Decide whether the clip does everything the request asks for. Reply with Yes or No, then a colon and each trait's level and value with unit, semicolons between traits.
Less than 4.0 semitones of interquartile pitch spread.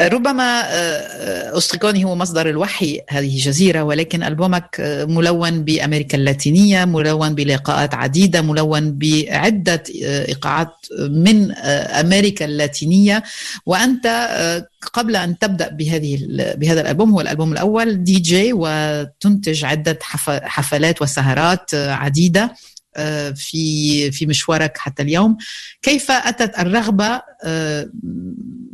No: average, 5.1 semitones